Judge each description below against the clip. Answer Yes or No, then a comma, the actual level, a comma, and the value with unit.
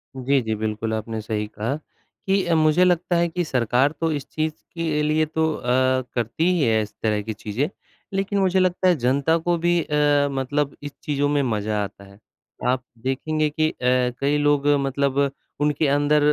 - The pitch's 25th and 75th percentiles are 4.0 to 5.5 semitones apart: Yes, average, 4.4 semitones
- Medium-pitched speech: Yes, medium, 145 Hz